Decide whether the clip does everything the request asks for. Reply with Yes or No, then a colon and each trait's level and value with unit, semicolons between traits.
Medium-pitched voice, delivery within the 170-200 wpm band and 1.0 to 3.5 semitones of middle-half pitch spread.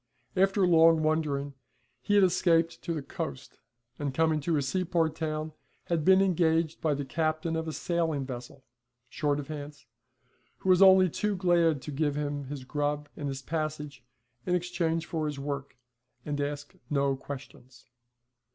No: medium, 155 Hz; average, 160 wpm; average, 2.8 semitones